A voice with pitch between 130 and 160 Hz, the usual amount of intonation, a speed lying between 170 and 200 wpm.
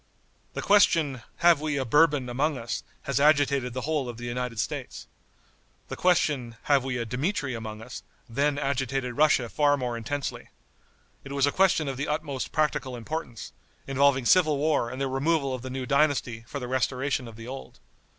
Yes: low, 135 Hz; average, 3.1 semitones; average, 180 wpm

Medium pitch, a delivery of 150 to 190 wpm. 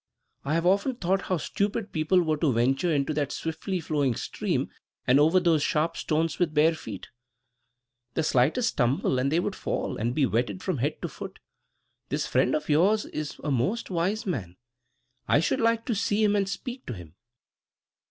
Yes: medium, 160 Hz; average, 185 wpm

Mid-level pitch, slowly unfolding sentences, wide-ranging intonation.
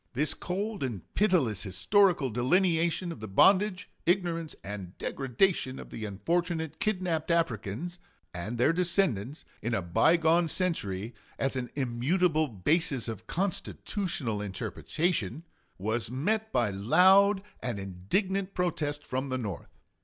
Yes: medium, 150 Hz; slow, 125 wpm; wide, 8.3 semitones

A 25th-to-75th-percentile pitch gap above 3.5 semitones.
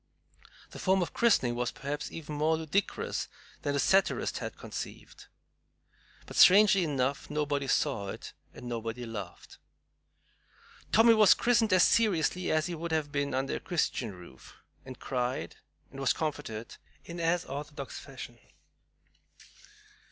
Yes: average, 5.3 semitones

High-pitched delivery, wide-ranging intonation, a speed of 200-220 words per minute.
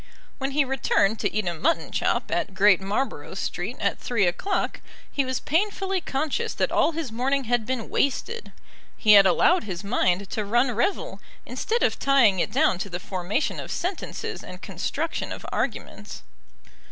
No: high, 245 Hz; wide, 6.7 semitones; average, 170 wpm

